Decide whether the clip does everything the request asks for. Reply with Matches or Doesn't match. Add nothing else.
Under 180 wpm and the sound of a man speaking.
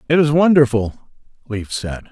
Matches